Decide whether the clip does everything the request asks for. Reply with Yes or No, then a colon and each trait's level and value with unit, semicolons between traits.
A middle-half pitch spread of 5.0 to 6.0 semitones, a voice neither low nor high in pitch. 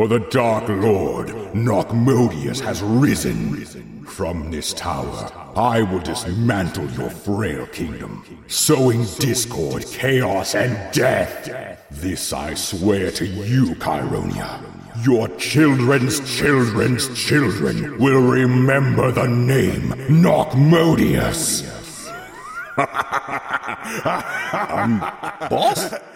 No: wide, 5.4 semitones; low, 120 Hz